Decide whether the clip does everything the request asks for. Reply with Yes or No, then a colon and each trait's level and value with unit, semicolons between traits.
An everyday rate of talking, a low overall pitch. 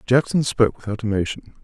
Yes: average, 145 wpm; low, 115 Hz